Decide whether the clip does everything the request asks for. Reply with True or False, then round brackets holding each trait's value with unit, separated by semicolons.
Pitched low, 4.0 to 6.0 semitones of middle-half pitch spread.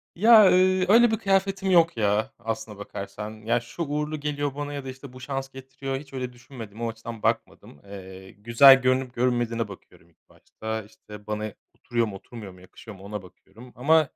True (125 Hz; 5.3 semitones)